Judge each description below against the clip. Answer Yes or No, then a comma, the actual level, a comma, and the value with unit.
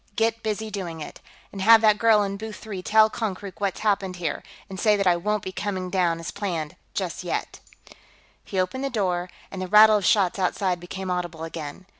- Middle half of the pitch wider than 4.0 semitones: No, average, 2.9 semitones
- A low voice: No, high, 195 Hz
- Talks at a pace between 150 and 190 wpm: No, fast, 205 wpm